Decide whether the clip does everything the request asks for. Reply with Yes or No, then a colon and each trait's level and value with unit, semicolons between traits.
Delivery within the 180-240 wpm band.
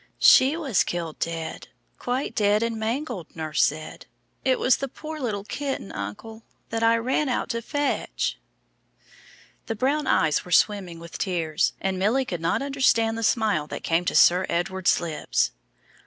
No: average, 160 wpm